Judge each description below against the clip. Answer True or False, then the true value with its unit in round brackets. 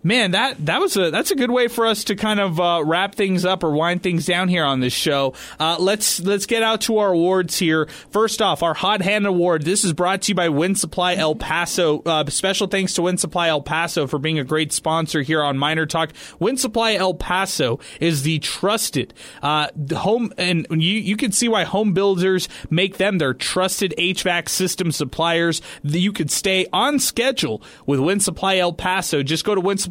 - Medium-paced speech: False (215 wpm)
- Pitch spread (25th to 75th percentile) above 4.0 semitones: False (3.6 semitones)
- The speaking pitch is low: False (180 Hz)